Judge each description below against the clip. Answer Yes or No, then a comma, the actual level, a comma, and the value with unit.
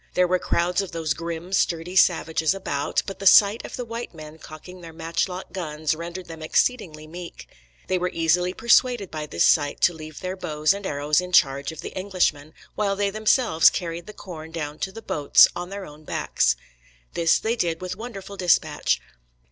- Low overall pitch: No, medium, 175 Hz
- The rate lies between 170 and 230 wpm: Yes, average, 190 wpm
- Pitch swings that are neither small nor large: Yes, average, 3.4 semitones